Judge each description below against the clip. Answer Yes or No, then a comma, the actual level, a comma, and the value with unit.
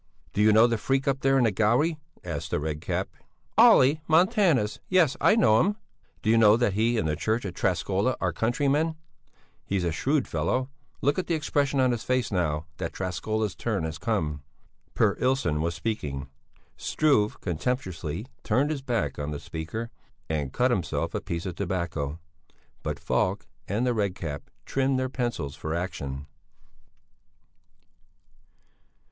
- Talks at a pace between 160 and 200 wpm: Yes, average, 165 wpm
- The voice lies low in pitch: Yes, low, 110 Hz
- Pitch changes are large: Yes, wide, 7.6 semitones